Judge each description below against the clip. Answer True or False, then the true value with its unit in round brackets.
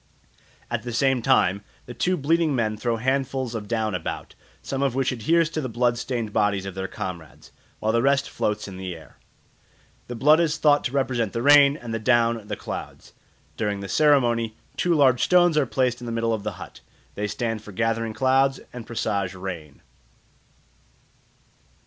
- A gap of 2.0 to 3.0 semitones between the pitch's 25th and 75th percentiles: False (4.2 semitones)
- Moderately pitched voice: False (120 Hz)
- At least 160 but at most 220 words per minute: True (185 wpm)